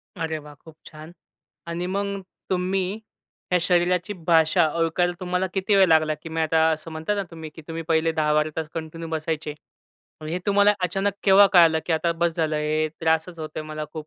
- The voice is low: No, medium, 165 Hz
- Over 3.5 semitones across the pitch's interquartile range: No, narrow, 2.4 semitones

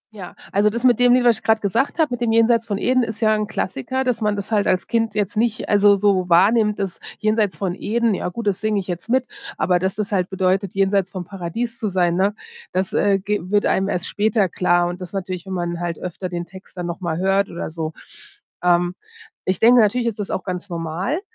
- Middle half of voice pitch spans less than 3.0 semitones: No, average, 3.4 semitones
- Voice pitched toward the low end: No, high, 200 Hz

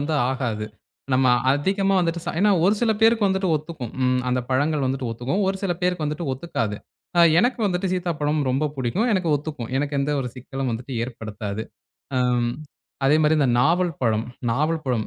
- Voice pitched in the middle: Yes, medium, 145 Hz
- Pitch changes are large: Yes, wide, 5.9 semitones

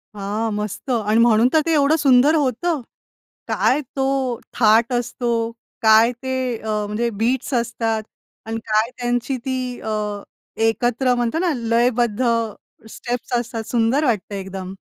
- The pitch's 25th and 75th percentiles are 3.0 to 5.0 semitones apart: No, narrow, 2.6 semitones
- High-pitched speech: Yes, high, 235 Hz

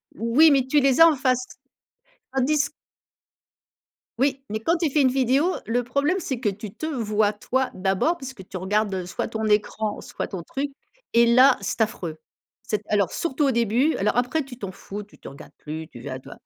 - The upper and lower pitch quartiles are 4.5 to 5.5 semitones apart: Yes, average, 5.0 semitones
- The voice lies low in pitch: No, high, 235 Hz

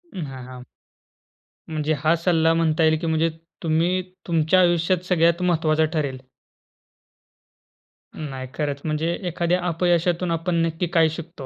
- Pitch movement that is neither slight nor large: No, narrow, 1.8 semitones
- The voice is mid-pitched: Yes, medium, 165 Hz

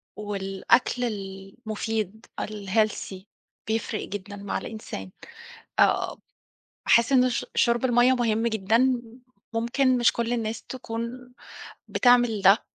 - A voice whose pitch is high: Yes, high, 225 Hz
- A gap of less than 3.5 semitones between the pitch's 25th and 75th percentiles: Yes, average, 2.9 semitones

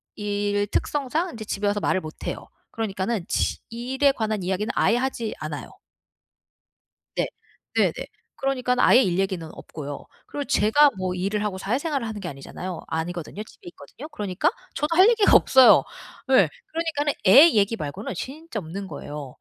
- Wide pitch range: Yes, wide, 6.1 semitones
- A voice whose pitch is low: No, high, 210 Hz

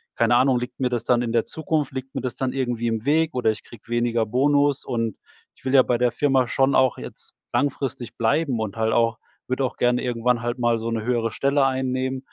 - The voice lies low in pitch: Yes, low, 125 Hz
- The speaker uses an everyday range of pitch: No, narrow, 2.2 semitones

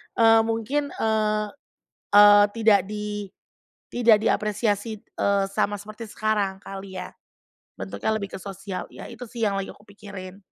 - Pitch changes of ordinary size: No, narrow, 2.0 semitones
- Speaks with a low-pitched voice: No, high, 210 Hz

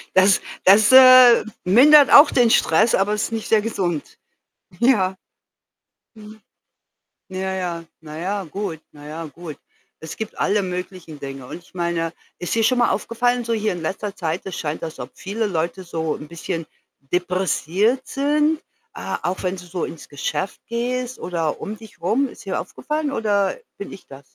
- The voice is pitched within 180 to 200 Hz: Yes, high, 190 Hz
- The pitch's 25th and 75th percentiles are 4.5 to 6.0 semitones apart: Yes, average, 5.2 semitones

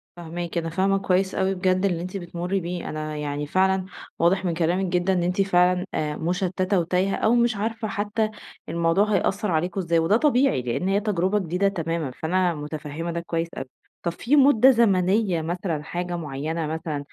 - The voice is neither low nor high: Yes, medium, 180 Hz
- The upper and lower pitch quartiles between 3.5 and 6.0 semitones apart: No, average, 2.9 semitones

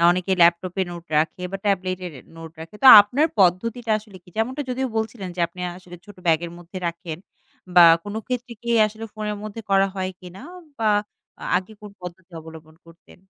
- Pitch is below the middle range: No, high, 190 Hz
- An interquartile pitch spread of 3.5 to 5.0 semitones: Yes, average, 3.9 semitones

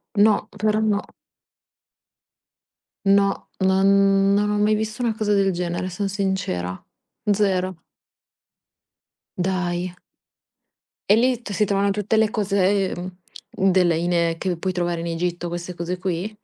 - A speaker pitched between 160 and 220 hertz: Yes, high, 190 Hz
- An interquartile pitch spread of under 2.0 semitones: No, average, 2.7 semitones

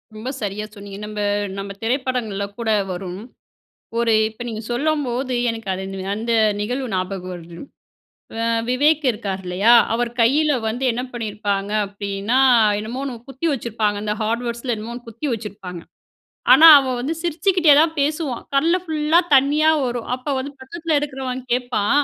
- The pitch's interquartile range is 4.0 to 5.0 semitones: Yes, average, 4.5 semitones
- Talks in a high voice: Yes, high, 235 Hz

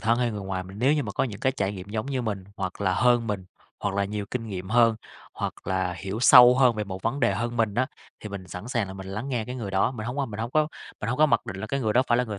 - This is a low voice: Yes, low, 110 Hz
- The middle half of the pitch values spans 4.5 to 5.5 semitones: No, average, 4.0 semitones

